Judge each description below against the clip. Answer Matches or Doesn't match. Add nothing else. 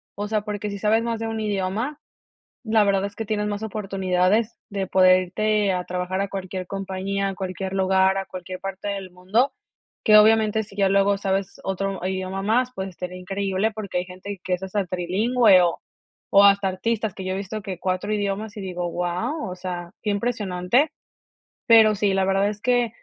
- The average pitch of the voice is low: Doesn't match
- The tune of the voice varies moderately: Doesn't match